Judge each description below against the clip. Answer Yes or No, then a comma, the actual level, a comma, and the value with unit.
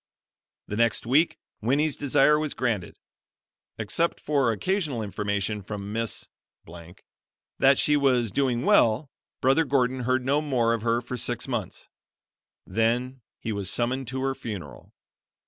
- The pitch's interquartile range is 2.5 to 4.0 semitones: Yes, average, 3.5 semitones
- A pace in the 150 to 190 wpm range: No, slow, 135 wpm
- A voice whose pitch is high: No, low, 125 Hz